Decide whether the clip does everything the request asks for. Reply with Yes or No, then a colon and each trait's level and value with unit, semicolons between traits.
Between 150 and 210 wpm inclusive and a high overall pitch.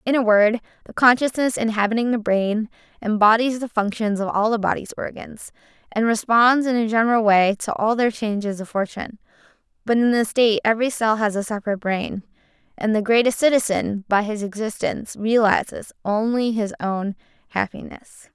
Yes: average, 165 wpm; high, 220 Hz